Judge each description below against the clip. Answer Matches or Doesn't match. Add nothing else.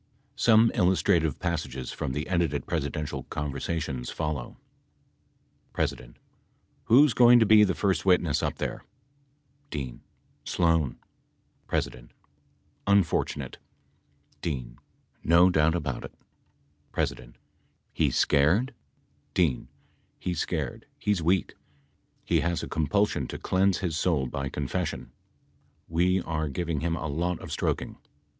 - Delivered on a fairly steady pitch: Doesn't match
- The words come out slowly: Matches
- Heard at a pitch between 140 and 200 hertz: Doesn't match